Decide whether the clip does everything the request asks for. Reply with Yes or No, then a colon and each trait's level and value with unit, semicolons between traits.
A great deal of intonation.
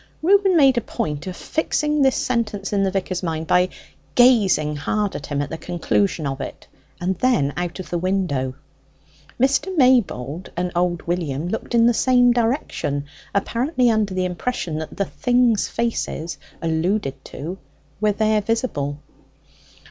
Yes: wide, 6.7 semitones